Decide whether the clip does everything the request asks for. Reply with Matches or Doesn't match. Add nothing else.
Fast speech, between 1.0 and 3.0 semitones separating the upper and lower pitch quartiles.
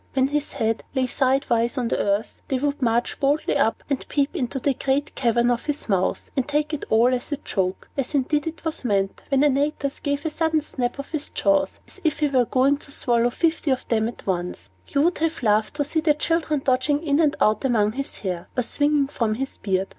Doesn't match